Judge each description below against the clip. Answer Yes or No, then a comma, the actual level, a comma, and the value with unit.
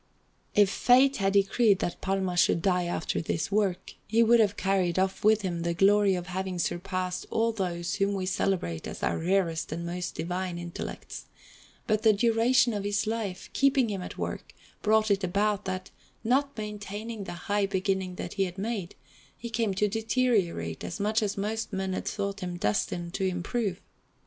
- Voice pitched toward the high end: Yes, high, 195 Hz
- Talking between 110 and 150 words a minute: No, average, 180 wpm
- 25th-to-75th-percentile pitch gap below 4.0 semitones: Yes, average, 3.0 semitones